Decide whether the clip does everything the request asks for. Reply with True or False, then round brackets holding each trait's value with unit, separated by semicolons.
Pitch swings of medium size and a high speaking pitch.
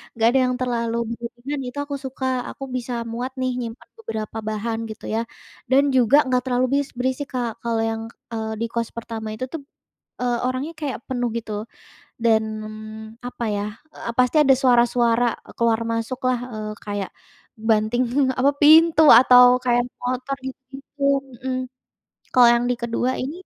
False (2.2 semitones; 245 Hz)